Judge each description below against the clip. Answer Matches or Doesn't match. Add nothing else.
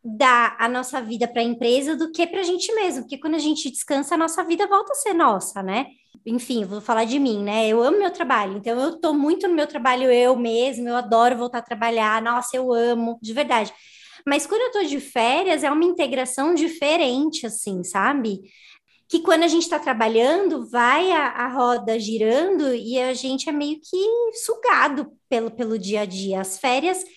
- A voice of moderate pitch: Doesn't match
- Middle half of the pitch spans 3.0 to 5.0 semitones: Doesn't match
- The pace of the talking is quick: Matches